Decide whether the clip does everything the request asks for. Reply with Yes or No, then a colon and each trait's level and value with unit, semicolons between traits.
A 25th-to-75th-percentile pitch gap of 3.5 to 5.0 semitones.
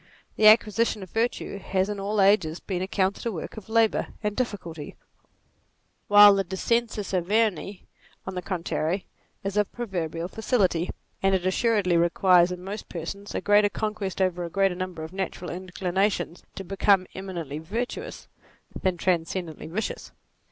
No: average, 2.7 semitones